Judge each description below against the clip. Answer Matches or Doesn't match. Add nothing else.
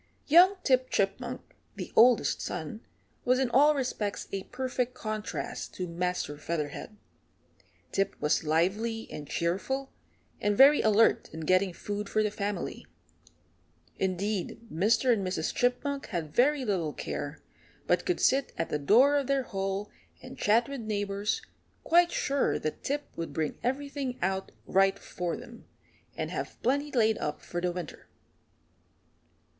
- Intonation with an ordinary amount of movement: Doesn't match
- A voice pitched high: Matches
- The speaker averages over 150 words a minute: Doesn't match